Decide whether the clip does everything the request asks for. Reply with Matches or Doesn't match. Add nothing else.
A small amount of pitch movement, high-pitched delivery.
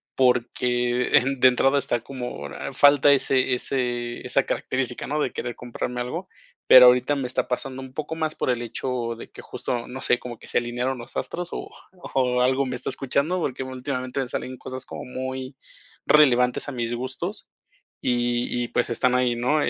Doesn't match